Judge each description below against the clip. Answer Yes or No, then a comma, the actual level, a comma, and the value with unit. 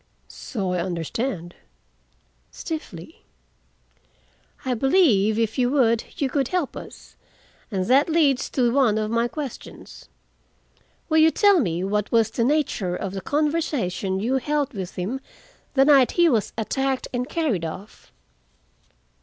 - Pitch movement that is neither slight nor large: No, wide, 6.3 semitones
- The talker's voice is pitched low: No, high, 245 Hz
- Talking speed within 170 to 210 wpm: No, slow, 135 wpm